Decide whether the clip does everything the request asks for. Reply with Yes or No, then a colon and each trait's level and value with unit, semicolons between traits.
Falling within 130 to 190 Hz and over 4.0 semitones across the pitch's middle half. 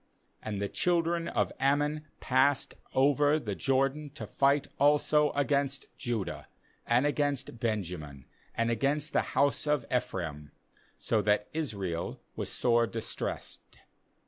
Yes: low, 135 Hz; average, 5.2 semitones